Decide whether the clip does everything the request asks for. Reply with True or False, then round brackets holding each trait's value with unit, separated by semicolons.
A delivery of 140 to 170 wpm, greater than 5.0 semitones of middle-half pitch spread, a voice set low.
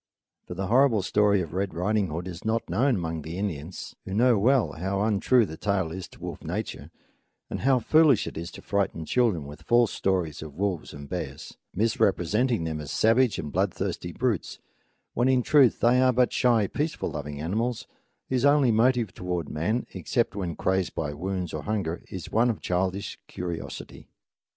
False (180 wpm; 5.6 semitones; 100 Hz)